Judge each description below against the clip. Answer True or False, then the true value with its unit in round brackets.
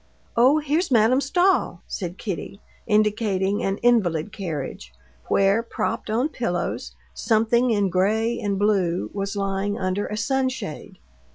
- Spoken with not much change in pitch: False (3.6 semitones)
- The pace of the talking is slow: True (125 wpm)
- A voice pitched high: True (210 Hz)